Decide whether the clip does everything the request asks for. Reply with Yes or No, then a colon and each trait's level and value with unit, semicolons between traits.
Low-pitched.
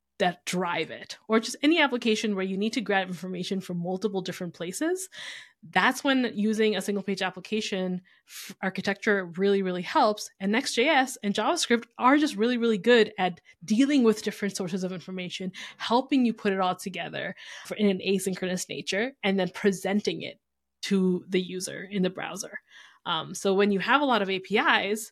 No: high, 200 Hz